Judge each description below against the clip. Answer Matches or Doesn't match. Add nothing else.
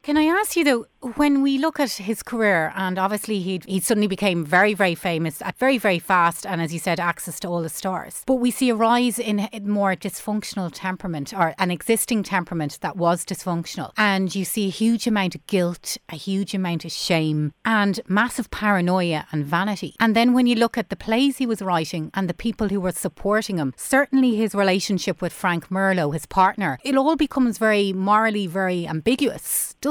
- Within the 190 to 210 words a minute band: Matches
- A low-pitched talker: Doesn't match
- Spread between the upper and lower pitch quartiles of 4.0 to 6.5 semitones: Matches